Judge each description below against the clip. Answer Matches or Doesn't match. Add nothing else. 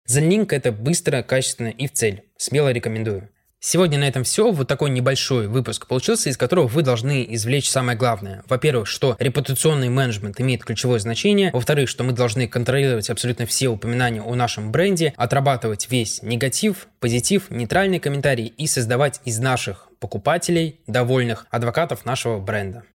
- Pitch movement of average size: Matches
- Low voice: Matches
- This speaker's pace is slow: Doesn't match